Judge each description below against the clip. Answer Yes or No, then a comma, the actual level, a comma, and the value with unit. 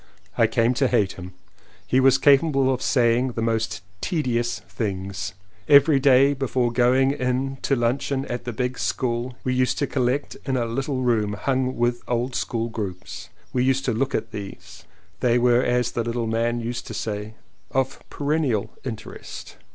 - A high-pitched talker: No, low, 125 Hz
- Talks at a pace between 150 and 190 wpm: Yes, average, 170 wpm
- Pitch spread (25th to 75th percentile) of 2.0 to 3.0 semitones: Yes, narrow, 2.4 semitones